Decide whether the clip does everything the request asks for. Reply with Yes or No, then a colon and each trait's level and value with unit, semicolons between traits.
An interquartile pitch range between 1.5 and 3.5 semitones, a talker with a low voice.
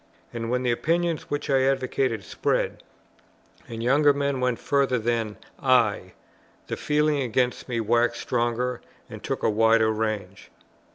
Yes: average, 3.1 semitones; low, 125 Hz